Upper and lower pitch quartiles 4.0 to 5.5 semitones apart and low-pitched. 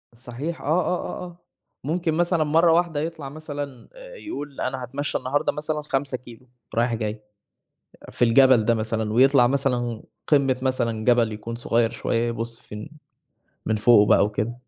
Yes: average, 4.3 semitones; low, 130 Hz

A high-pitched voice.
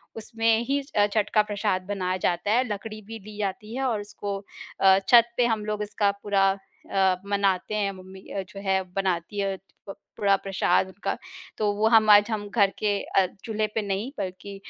Yes: high, 205 Hz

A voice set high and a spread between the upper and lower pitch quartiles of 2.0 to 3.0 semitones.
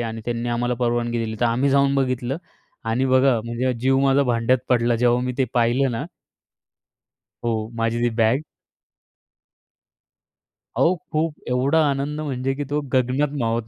No: low, 125 Hz; narrow, 2.5 semitones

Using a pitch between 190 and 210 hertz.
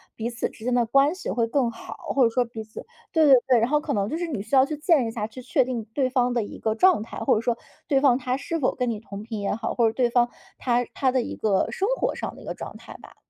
No: high, 245 Hz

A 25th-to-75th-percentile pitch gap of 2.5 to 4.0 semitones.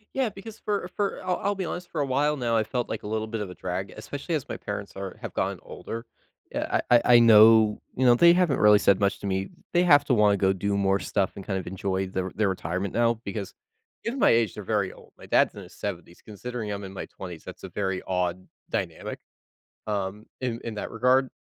No: average, 4.7 semitones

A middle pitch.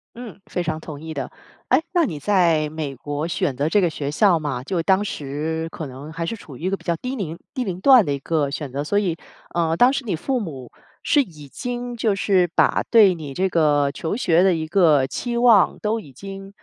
Yes: medium, 170 Hz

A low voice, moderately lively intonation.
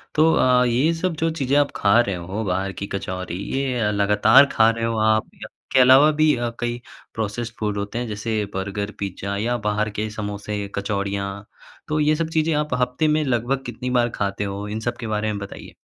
Yes: low, 110 Hz; average, 4.0 semitones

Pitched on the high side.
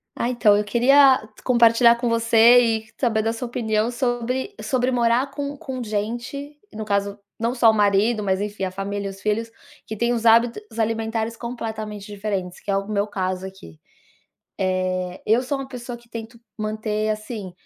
Yes: high, 225 Hz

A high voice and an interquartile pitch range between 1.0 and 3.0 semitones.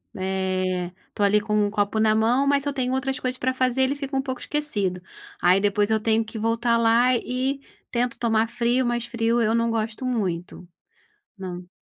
No: high, 230 Hz; average, 3.6 semitones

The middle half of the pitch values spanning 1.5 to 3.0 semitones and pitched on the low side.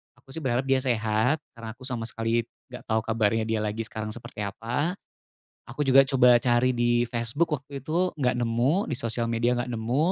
Yes: average, 2.7 semitones; low, 120 Hz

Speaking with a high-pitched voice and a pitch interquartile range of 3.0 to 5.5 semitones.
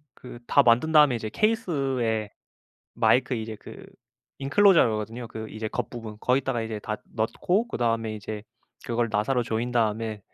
No: low, 115 Hz; average, 3.5 semitones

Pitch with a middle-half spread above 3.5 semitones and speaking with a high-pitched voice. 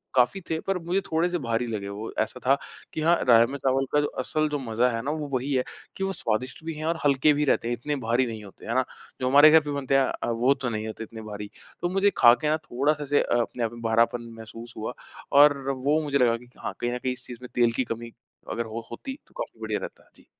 No: average, 4.1 semitones; low, 130 Hz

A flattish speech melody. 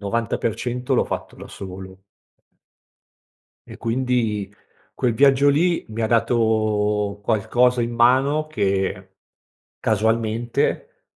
No: average, 3.2 semitones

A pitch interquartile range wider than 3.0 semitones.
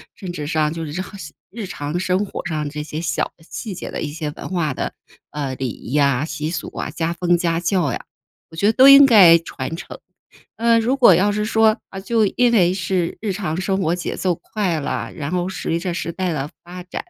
Yes: average, 3.9 semitones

